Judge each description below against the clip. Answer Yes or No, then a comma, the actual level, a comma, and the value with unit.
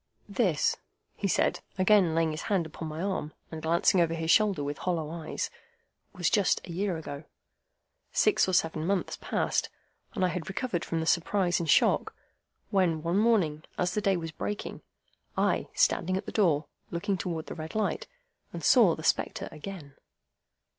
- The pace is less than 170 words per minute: No, average, 175 wpm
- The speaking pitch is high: No, medium, 175 Hz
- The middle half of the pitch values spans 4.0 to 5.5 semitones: No, average, 3.3 semitones